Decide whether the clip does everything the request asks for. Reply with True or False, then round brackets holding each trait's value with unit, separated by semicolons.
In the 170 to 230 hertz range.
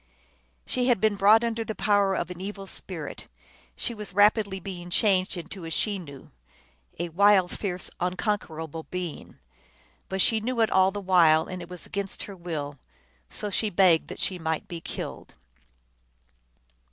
True (190 Hz)